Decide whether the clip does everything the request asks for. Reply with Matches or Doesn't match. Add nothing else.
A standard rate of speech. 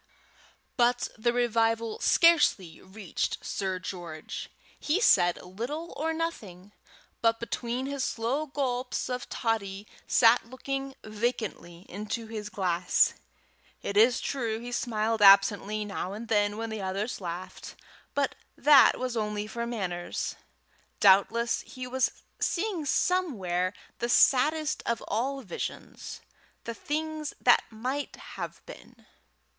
Doesn't match